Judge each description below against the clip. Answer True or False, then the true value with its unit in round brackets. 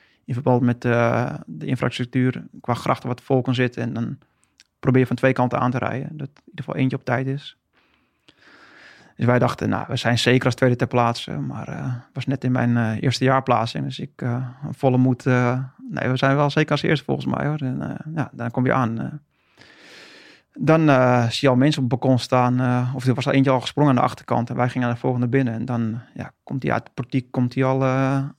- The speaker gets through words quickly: True (240 wpm)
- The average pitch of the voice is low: True (130 Hz)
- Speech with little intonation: True (1.7 semitones)